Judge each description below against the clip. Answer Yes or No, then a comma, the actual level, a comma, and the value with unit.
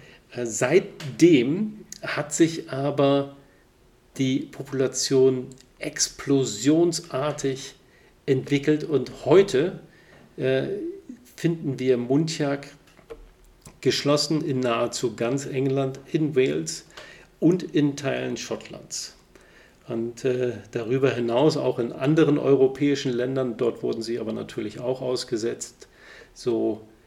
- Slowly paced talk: Yes, slow, 90 wpm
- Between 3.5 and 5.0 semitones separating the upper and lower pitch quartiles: No, average, 2.7 semitones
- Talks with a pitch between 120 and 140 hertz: Yes, low, 135 Hz